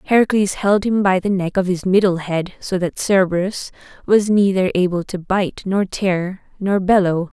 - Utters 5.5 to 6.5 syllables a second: No, 4.6 syllables/s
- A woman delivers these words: Yes, female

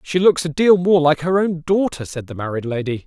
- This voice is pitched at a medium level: Yes, medium, 160 Hz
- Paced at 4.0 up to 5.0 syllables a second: No, 5.4 syllables/s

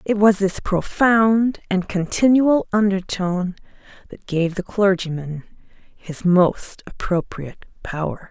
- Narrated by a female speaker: Yes, female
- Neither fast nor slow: No, slow, 110 wpm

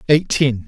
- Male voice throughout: Yes, male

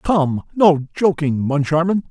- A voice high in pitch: No, medium, 160 Hz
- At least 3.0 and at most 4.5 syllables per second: Yes, 3.9 syllables/s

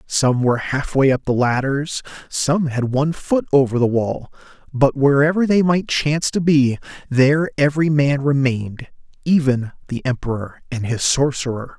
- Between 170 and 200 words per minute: No, average, 160 wpm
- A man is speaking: Yes, male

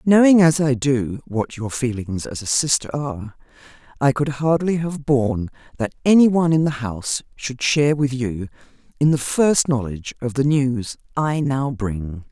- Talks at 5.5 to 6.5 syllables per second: No, 4.7 syllables/s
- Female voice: Yes, female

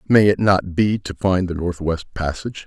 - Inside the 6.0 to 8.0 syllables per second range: No, 5.0 syllables/s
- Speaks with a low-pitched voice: Yes, very low, 95 Hz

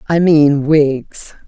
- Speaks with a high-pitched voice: No, medium, 150 Hz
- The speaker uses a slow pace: Yes, slow, 120 wpm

